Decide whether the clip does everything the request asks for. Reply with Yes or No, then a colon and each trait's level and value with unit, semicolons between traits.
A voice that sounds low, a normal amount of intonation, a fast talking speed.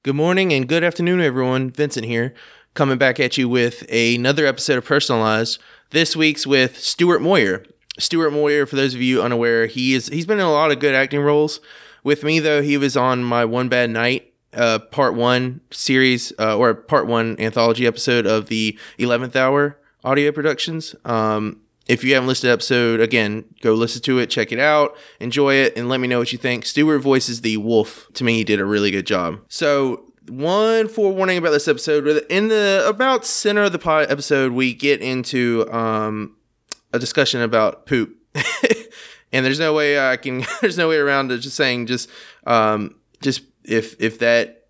No: low, 130 Hz; average, 4.1 semitones; average, 190 wpm